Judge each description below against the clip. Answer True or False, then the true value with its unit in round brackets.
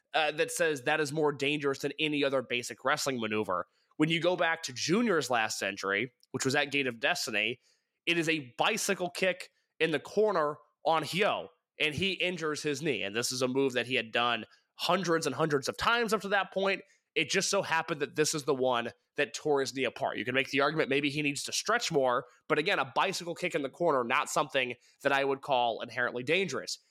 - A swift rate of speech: True (225 wpm)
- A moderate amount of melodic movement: True (4.1 semitones)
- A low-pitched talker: False (145 Hz)